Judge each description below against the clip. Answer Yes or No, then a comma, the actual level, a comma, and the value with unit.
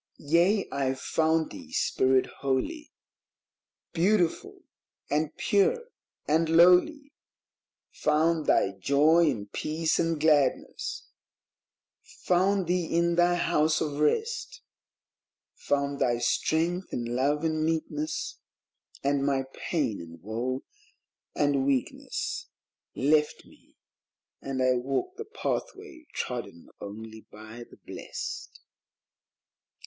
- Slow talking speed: Yes, slow, 100 wpm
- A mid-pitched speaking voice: Yes, medium, 155 Hz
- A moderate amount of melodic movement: Yes, average, 4.8 semitones